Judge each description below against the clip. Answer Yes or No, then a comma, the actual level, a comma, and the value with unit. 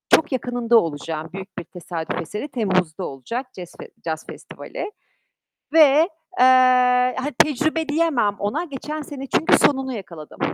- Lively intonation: Yes, wide, 8.6 semitones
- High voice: Yes, high, 240 Hz